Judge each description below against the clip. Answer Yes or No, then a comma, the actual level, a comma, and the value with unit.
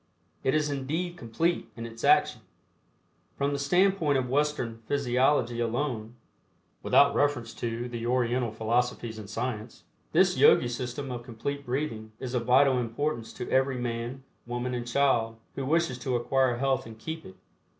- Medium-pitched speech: No, low, 125 Hz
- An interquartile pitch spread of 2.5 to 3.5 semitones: Yes, average, 3.2 semitones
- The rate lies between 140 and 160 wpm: Yes, average, 155 wpm